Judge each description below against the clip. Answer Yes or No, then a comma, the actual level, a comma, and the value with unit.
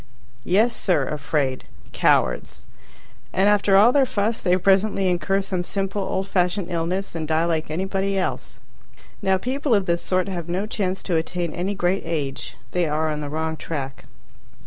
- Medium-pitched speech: Yes, medium, 180 Hz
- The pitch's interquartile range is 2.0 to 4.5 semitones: Yes, average, 3.3 semitones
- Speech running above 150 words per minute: Yes, average, 170 wpm